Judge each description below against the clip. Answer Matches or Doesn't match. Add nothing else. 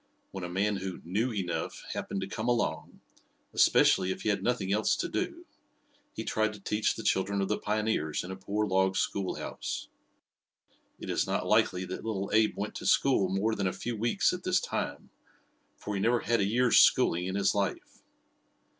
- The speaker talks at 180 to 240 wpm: Matches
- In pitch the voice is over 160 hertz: Doesn't match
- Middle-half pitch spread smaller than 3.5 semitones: Matches